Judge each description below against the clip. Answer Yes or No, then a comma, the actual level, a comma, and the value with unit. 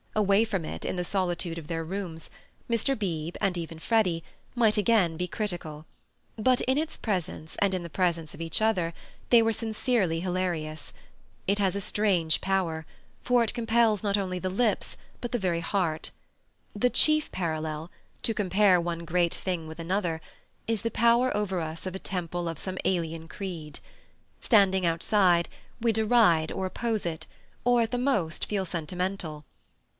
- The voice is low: No, medium, 185 Hz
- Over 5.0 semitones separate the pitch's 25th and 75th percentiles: No, average, 4.5 semitones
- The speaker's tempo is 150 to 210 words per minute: Yes, average, 165 wpm